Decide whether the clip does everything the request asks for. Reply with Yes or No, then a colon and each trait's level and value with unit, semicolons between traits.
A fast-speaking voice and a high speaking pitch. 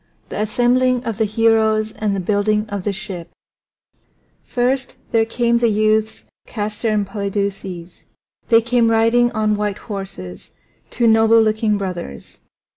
No: slow, 135 wpm; high, 215 Hz